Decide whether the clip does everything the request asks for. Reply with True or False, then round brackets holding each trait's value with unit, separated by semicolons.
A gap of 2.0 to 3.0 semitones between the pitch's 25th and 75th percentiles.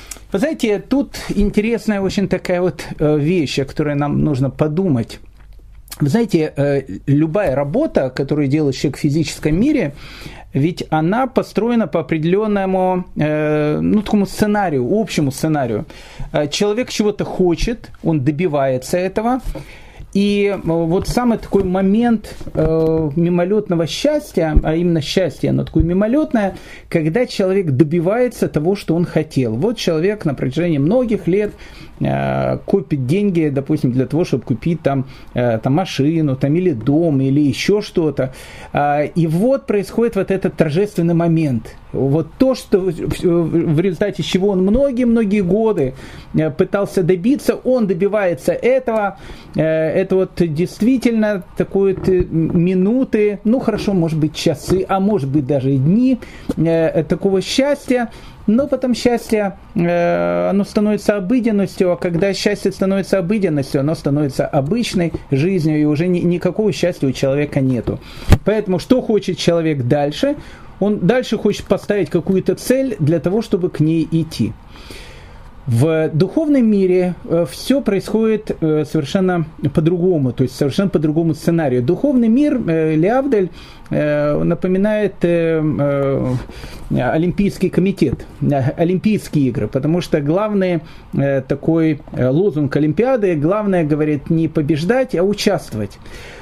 False (5.1 semitones)